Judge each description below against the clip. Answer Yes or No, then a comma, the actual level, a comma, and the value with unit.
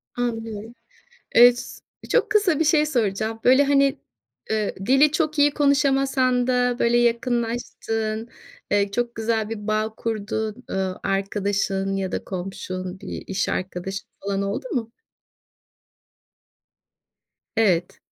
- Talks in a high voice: Yes, high, 225 Hz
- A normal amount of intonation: Yes, average, 4.1 semitones